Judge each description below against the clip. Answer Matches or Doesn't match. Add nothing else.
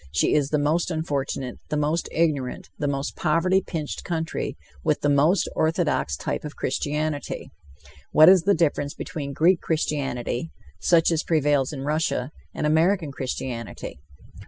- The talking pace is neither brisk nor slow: Matches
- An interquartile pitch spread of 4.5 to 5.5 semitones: Doesn't match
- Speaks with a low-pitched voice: Doesn't match